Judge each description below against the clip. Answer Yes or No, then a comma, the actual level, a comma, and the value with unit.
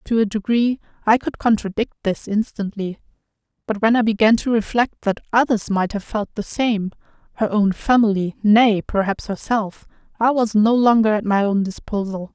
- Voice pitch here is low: No, high, 215 Hz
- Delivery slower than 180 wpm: Yes, average, 160 wpm